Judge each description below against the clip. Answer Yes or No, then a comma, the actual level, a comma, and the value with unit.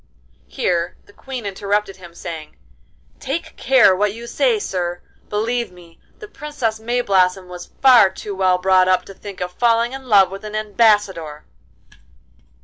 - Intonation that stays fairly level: No, average, 4.5 semitones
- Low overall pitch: No, high, 205 Hz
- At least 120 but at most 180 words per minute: Yes, average, 150 wpm